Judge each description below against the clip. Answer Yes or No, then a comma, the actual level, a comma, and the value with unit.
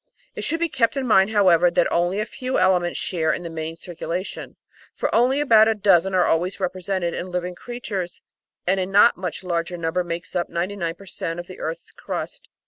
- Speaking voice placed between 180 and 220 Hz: Yes, medium, 185 Hz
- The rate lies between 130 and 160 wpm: No, fast, 205 wpm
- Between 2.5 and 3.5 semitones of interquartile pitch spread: Yes, average, 2.8 semitones